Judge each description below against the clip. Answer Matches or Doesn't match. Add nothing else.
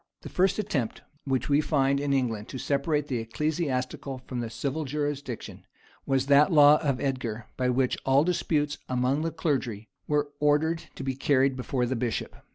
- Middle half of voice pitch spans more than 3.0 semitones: Doesn't match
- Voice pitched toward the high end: Doesn't match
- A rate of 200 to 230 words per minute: Doesn't match